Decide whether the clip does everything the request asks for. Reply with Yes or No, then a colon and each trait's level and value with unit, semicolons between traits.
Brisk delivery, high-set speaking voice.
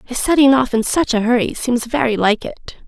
Yes: fast, 230 wpm; high, 245 Hz